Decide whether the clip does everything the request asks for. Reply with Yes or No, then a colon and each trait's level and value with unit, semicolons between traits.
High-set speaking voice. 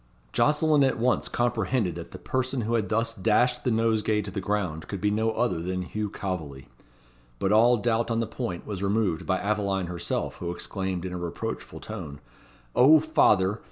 No: low, 105 Hz